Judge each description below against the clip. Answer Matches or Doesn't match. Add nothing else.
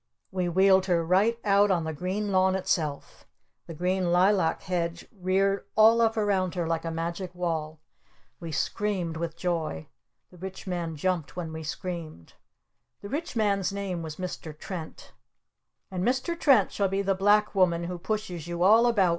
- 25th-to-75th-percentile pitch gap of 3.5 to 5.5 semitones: Doesn't match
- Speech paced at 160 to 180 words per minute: Matches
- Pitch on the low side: Doesn't match